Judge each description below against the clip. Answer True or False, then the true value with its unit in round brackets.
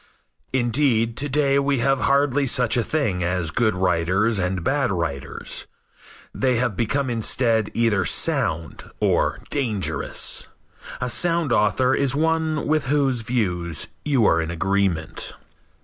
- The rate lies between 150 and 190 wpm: False (135 wpm)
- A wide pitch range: True (6.5 semitones)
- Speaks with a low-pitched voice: True (120 Hz)